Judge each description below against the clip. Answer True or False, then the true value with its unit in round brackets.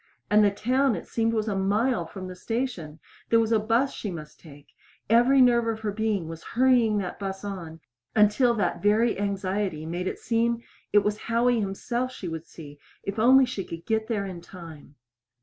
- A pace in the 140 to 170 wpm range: False (195 wpm)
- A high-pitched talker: True (210 Hz)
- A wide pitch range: False (4.1 semitones)